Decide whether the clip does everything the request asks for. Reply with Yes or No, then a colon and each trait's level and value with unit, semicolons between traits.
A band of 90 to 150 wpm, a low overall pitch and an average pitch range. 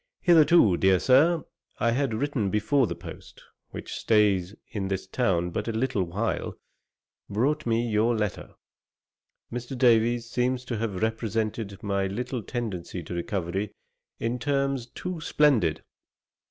Yes: slow, 135 wpm; low, 115 Hz; average, 4.4 semitones